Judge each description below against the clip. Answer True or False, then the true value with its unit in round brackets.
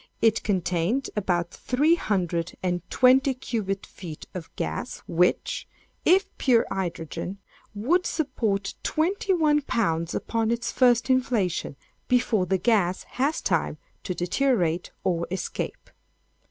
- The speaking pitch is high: True (215 Hz)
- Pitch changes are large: True (6.4 semitones)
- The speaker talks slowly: True (120 wpm)